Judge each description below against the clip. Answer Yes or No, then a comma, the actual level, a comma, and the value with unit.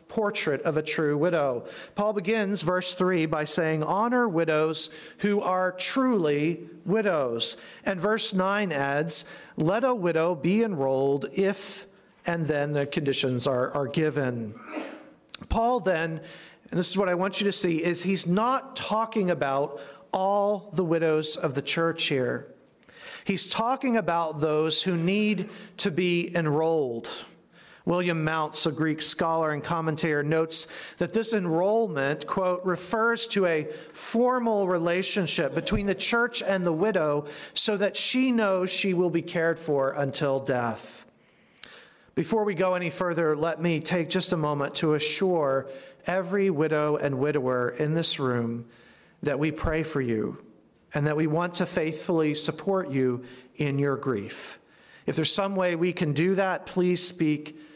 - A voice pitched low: No, medium, 170 Hz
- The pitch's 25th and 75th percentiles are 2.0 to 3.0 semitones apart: No, average, 4.3 semitones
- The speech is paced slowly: No, average, 150 wpm